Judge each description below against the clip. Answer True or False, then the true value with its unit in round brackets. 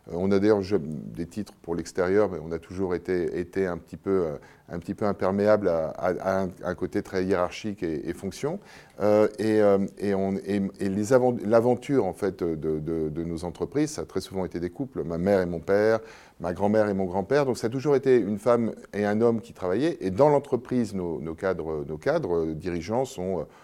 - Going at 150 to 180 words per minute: False (220 wpm)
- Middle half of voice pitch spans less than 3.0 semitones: False (3.4 semitones)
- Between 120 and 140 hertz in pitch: False (95 Hz)